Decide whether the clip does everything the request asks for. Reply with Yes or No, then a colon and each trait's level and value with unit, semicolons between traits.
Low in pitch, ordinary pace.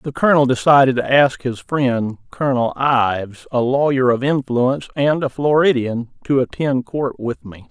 Yes: low, 130 Hz; average, 165 wpm